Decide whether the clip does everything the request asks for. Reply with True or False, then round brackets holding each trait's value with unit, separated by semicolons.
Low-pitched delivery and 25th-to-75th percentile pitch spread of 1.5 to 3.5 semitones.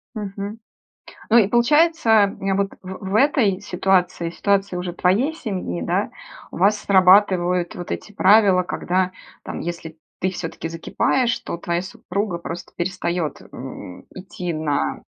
False (185 Hz; 2.9 semitones)